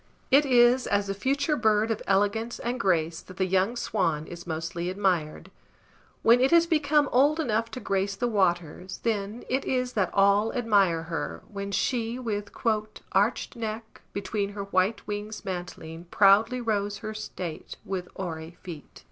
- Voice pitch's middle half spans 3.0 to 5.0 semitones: Yes, average, 4.0 semitones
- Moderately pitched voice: No, high, 205 Hz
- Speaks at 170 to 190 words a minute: No, average, 160 wpm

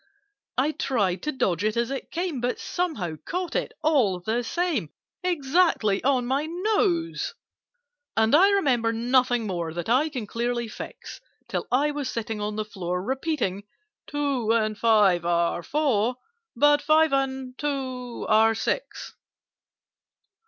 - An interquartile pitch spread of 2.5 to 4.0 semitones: No, wide, 5.5 semitones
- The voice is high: Yes, very high, 250 Hz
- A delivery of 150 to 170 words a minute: No, average, 140 wpm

